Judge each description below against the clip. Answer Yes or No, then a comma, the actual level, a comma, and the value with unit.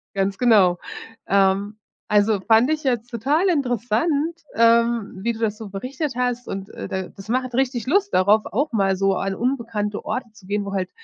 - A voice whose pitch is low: No, high, 225 Hz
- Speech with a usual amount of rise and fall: Yes, average, 4.1 semitones